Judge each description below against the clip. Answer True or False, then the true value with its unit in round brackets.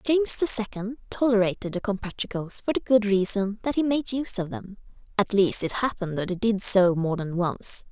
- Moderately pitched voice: False (210 Hz)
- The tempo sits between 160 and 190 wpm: False (205 wpm)